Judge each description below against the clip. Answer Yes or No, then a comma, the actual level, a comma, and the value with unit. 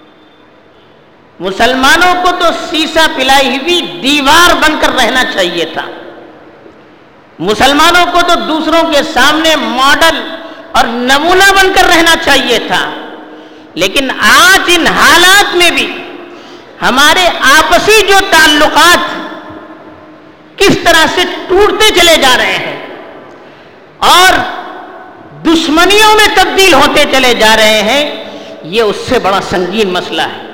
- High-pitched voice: Yes, very high, 330 Hz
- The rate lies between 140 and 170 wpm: No, average, 120 wpm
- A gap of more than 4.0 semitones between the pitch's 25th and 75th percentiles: Yes, average, 4.8 semitones